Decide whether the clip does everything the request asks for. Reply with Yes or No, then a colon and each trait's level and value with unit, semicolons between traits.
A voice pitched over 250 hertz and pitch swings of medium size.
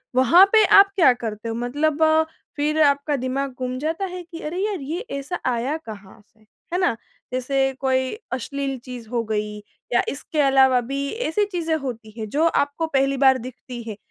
Yes: very high, 270 Hz; average, 4.1 semitones